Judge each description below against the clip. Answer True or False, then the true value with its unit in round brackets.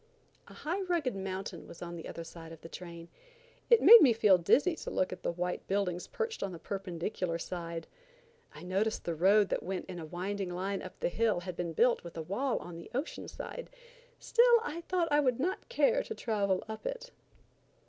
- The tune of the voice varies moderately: False (8.2 semitones)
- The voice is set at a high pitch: True (195 Hz)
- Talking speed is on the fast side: True (210 wpm)